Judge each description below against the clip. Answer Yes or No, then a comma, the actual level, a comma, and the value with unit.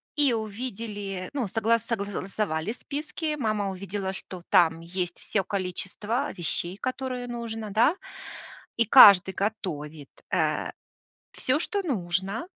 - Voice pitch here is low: No, high, 205 Hz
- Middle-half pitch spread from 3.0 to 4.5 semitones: Yes, average, 4.2 semitones